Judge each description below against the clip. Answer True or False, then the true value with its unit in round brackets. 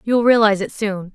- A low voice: False (210 Hz)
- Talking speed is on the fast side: True (265 wpm)